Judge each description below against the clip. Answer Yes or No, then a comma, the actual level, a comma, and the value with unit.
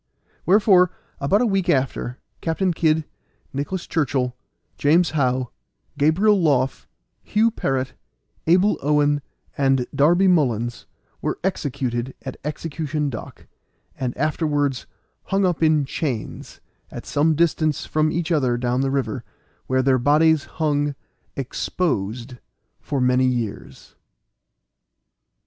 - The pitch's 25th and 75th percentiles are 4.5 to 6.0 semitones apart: No, average, 4.0 semitones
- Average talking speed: No, slow, 115 wpm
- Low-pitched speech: No, medium, 145 Hz